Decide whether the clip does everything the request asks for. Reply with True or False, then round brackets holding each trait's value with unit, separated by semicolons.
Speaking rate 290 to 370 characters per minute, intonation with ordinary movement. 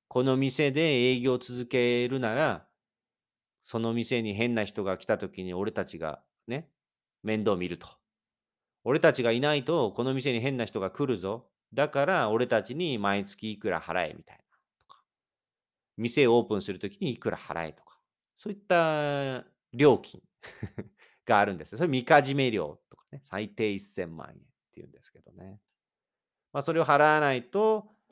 True (295 characters per minute; 5.0 semitones)